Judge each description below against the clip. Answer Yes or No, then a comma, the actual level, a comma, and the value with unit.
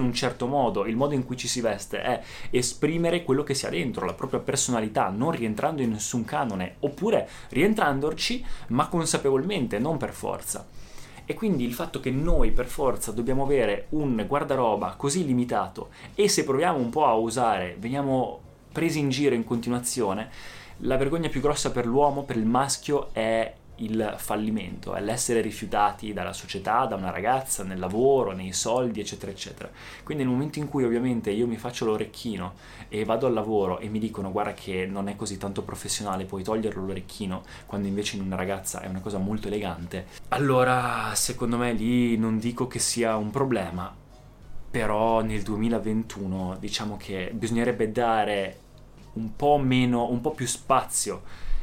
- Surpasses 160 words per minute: Yes, fast, 170 wpm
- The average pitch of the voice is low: Yes, low, 115 Hz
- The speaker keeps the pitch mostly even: No, average, 4.1 semitones